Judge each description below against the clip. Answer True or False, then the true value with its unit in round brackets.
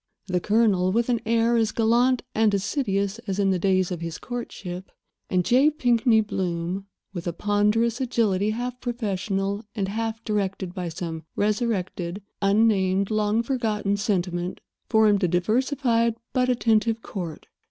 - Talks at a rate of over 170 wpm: False (140 wpm)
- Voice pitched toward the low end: False (210 Hz)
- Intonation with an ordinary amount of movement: True (3.6 semitones)